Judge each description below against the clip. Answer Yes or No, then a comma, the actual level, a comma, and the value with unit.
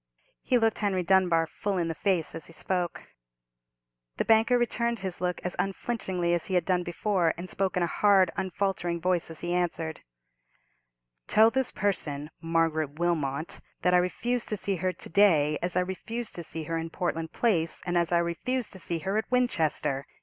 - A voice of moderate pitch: Yes, medium, 180 Hz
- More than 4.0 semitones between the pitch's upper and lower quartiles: No, average, 3.4 semitones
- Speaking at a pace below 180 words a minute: No, average, 190 wpm